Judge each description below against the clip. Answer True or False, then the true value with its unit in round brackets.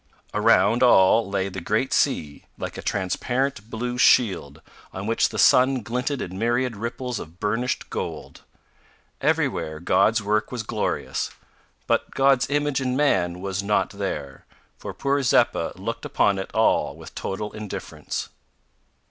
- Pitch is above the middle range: False (110 Hz)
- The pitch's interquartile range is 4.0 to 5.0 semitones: True (4.6 semitones)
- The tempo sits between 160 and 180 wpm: False (140 wpm)